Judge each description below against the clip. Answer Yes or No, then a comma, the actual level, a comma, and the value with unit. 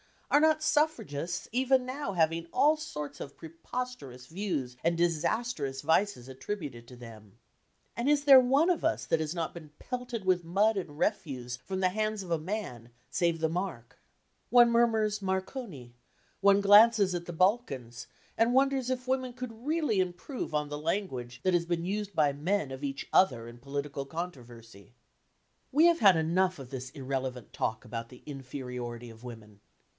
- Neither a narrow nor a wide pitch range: No, wide, 8.8 semitones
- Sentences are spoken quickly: No, average, 170 wpm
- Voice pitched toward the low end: No, medium, 175 Hz